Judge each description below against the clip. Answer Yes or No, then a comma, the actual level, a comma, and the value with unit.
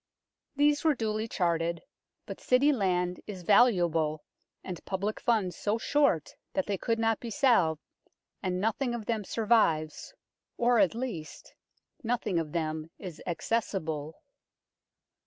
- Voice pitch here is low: No, high, 200 Hz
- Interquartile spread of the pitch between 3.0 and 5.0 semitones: No, wide, 5.6 semitones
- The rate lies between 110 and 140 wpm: Yes, slow, 135 wpm